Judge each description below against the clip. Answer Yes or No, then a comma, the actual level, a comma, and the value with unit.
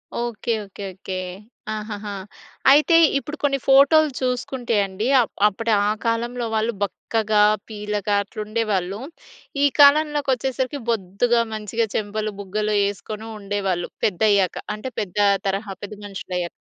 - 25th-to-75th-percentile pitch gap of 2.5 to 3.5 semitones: Yes, average, 3.2 semitones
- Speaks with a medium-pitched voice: No, high, 215 Hz